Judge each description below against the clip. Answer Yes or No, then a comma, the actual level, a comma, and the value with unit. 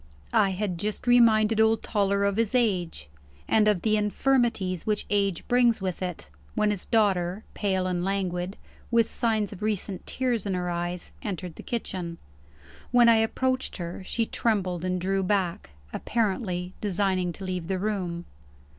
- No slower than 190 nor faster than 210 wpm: No, average, 160 wpm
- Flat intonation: No, average, 3.3 semitones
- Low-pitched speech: No, high, 200 Hz